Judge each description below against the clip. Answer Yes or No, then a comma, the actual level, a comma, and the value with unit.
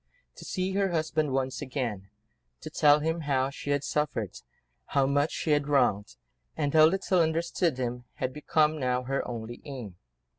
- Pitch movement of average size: Yes, average, 3.6 semitones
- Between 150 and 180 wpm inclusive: Yes, average, 170 wpm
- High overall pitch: No, medium, 145 Hz